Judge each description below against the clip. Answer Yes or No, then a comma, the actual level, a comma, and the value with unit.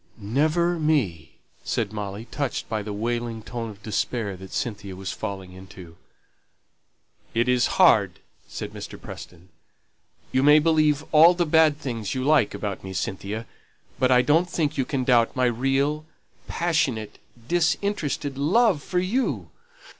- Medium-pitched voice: No, low, 125 Hz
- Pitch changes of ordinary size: No, wide, 6.6 semitones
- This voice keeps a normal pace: Yes, average, 145 wpm